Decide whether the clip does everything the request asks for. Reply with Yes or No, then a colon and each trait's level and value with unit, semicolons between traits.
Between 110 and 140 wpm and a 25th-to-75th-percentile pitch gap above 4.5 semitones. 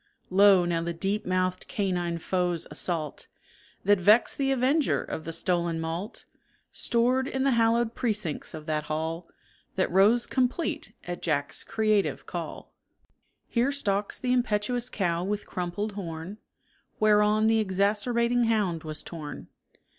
Yes: slow, 135 wpm; average, 5.1 semitones